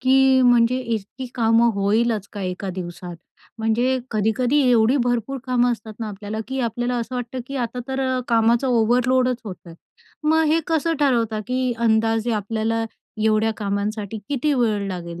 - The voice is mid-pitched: No, high, 230 Hz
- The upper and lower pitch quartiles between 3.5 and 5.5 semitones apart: No, average, 2.8 semitones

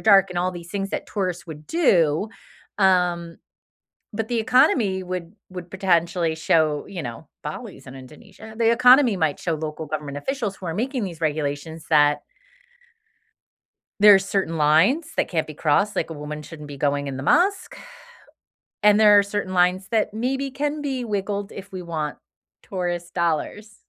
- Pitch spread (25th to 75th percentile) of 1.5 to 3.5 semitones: No, average, 4.9 semitones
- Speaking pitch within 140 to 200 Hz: Yes, medium, 185 Hz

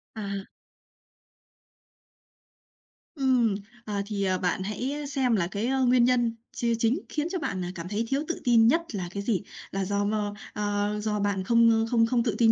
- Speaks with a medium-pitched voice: No, high, 220 Hz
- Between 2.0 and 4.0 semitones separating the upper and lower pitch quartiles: Yes, average, 3.5 semitones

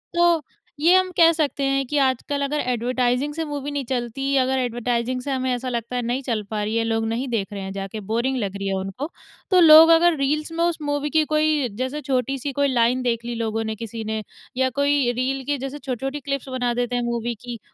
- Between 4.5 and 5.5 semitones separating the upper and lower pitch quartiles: No, average, 3.5 semitones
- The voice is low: No, very high, 255 Hz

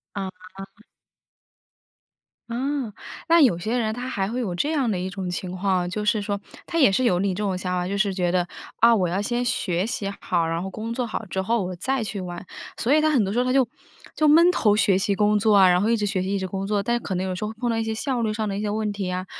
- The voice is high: Yes, high, 205 Hz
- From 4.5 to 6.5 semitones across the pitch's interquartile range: No, average, 3.9 semitones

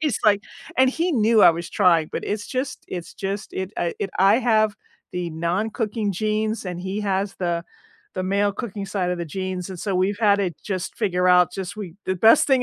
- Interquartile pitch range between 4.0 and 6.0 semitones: No, average, 3.0 semitones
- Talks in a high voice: Yes, high, 195 Hz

